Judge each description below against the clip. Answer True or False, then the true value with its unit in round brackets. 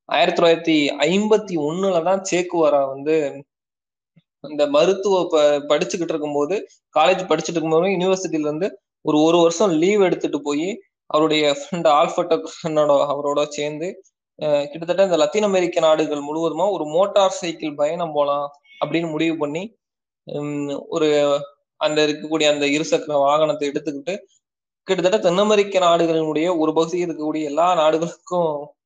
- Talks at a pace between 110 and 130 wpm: True (120 wpm)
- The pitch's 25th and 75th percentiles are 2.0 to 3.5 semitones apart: True (3.2 semitones)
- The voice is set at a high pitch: False (155 Hz)